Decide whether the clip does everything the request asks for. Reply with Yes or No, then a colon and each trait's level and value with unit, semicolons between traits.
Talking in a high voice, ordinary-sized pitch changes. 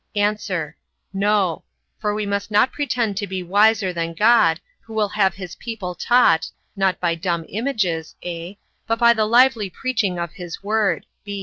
Yes: high, 200 Hz; average, 3.7 semitones